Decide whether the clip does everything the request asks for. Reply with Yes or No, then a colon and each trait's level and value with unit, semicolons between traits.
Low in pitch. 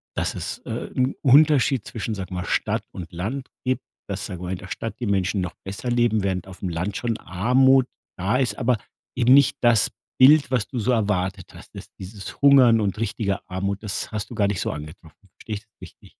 Yes: low, 105 Hz